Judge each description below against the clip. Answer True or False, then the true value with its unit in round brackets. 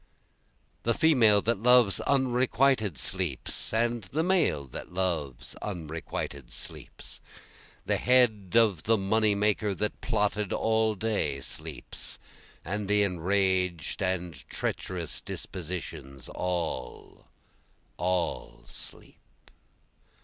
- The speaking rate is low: True (100 wpm)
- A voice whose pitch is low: True (100 Hz)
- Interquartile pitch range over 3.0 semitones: True (4.3 semitones)